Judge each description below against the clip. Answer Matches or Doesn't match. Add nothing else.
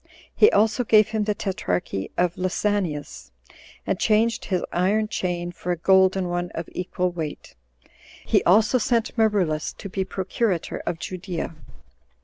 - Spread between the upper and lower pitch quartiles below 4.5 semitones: Matches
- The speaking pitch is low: Doesn't match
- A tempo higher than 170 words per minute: Doesn't match